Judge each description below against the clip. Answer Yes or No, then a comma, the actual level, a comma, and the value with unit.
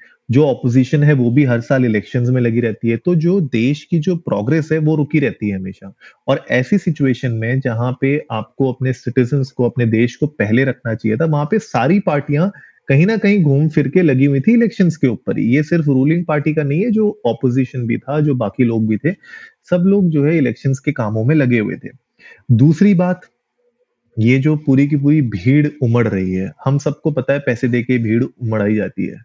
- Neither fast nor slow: No, fast, 215 wpm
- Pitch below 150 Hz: Yes, medium, 140 Hz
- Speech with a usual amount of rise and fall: Yes, average, 4.6 semitones